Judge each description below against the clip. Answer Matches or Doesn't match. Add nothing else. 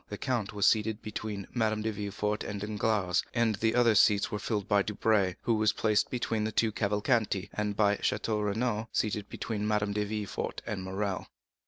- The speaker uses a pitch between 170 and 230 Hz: Doesn't match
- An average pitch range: Doesn't match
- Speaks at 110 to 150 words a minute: Doesn't match